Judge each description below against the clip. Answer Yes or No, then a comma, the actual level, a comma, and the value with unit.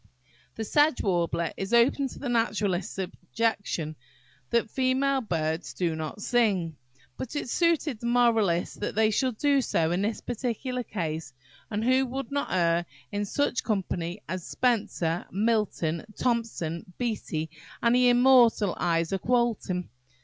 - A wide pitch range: Yes, wide, 5.9 semitones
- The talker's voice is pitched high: Yes, high, 215 Hz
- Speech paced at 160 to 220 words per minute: No, average, 140 wpm